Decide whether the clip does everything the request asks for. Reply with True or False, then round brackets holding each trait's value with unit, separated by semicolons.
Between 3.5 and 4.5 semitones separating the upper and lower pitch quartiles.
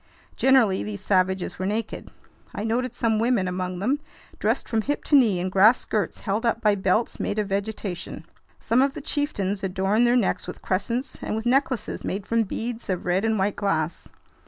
True (3.8 semitones)